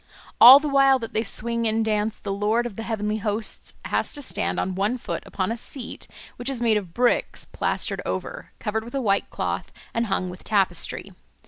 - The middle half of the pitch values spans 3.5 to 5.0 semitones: No, narrow, 2.5 semitones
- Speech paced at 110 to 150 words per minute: No, fast, 205 wpm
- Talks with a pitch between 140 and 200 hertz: No, high, 225 Hz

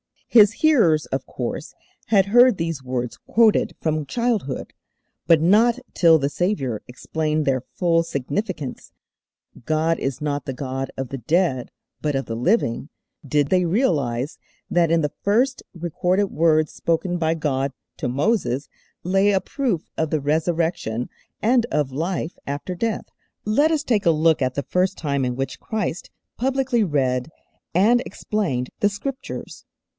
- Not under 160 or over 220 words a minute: No, average, 150 wpm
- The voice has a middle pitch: Yes, medium, 165 Hz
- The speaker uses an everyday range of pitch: No, wide, 6.6 semitones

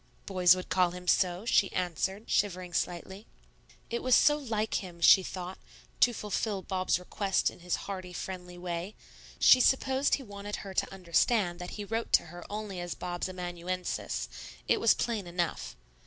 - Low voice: No, medium, 185 Hz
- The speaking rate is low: No, average, 170 wpm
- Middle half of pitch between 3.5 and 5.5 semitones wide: No, average, 2.7 semitones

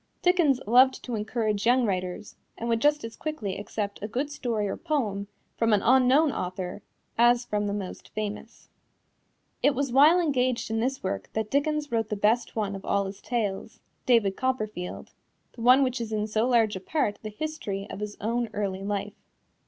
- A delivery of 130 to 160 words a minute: No, average, 185 wpm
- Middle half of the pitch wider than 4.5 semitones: No, average, 3.9 semitones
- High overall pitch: Yes, high, 225 Hz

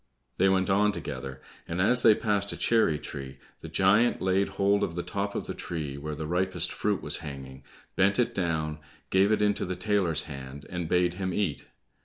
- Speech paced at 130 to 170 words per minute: No, average, 200 wpm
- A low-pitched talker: Yes, very low, 90 Hz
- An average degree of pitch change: Yes, average, 4.6 semitones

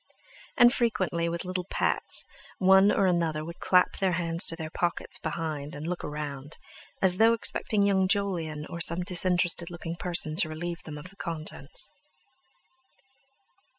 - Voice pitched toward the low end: No, medium, 170 Hz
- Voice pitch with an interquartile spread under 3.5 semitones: Yes, average, 2.8 semitones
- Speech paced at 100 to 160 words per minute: Yes, average, 150 wpm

